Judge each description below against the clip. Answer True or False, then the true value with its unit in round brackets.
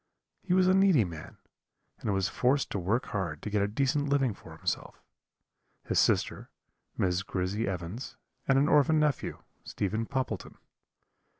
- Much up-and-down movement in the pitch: True (6.7 semitones)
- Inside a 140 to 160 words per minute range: True (155 wpm)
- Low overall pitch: True (115 Hz)